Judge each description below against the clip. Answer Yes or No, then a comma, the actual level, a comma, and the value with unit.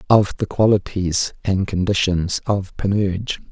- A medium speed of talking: No, slow, 120 wpm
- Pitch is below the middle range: Yes, very low, 95 Hz